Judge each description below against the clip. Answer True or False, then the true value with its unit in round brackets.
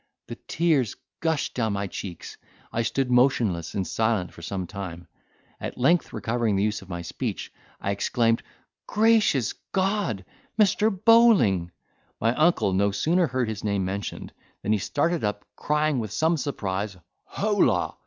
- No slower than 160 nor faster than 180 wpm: False (145 wpm)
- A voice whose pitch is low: True (115 Hz)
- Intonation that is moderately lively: False (8.1 semitones)